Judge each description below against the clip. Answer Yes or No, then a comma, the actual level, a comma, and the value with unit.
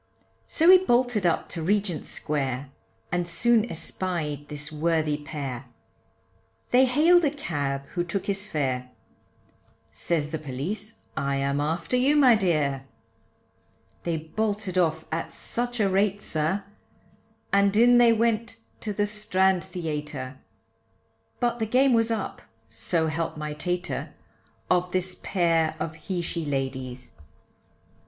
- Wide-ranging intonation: Yes, wide, 6.1 semitones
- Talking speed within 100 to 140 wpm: Yes, slow, 135 wpm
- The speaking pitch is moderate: Yes, medium, 175 Hz